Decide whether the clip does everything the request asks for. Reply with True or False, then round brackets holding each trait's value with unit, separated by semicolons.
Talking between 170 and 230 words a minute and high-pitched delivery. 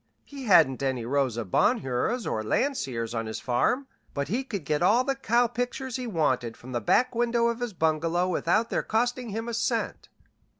True (185 wpm; 200 Hz)